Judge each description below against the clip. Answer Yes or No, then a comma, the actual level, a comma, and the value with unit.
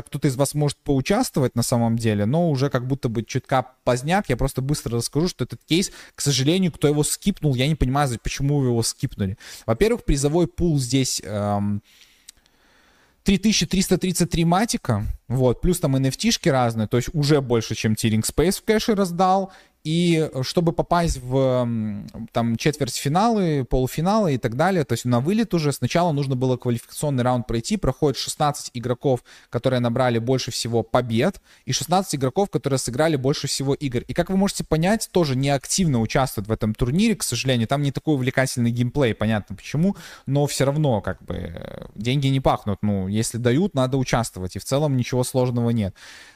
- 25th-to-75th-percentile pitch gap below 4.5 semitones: No, average, 4.9 semitones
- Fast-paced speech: Yes, fast, 170 wpm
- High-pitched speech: No, low, 135 Hz